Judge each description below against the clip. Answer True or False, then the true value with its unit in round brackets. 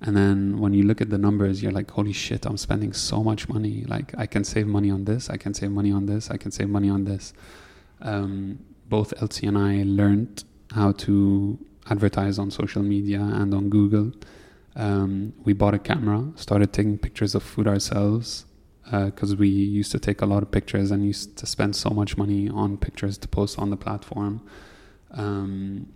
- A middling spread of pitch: False (0.9 semitones)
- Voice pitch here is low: True (100 Hz)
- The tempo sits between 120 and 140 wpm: False (200 wpm)